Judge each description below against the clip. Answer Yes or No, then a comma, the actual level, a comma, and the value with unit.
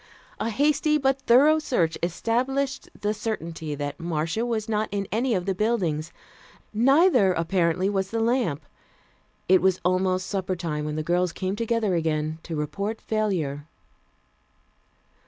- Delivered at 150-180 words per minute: No, average, 140 wpm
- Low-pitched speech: No, high, 195 Hz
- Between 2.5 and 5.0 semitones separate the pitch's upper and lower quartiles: No, wide, 5.5 semitones